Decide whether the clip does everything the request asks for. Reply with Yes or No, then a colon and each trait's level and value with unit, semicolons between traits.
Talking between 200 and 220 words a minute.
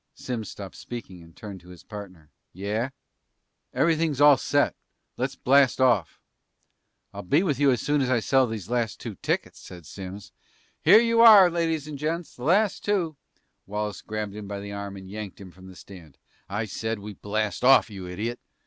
No: average, 190 wpm